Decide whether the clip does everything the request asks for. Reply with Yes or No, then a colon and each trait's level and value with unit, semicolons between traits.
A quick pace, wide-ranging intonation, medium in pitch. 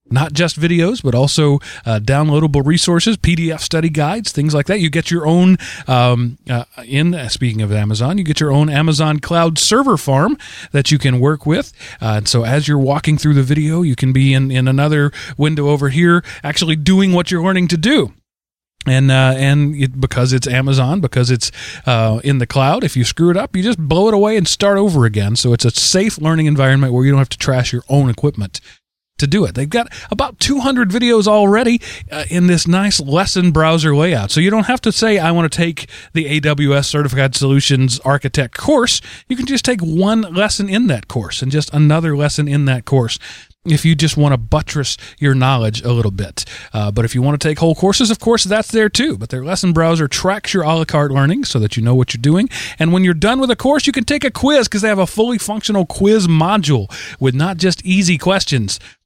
Yes: fast, 225 wpm; wide, 5.8 semitones; medium, 150 Hz